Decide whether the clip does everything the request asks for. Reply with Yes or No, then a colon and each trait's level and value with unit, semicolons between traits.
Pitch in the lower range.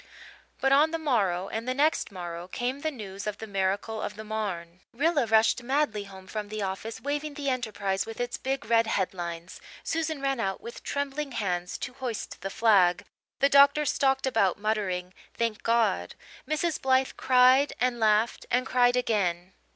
No: high, 225 Hz